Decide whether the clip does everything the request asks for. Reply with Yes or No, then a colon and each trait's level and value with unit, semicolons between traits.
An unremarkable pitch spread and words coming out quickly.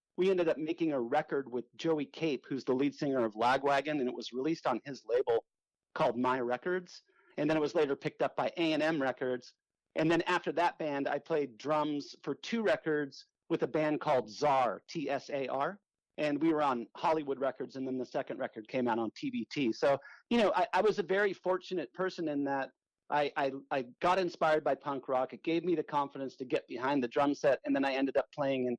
Yes: average, 4.5 semitones; fast, 230 wpm